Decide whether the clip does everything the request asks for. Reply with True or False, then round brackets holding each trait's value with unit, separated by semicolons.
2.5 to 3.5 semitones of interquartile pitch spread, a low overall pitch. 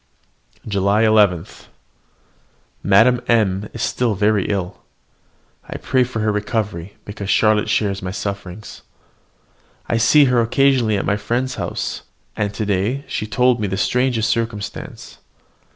True (2.8 semitones; 105 Hz)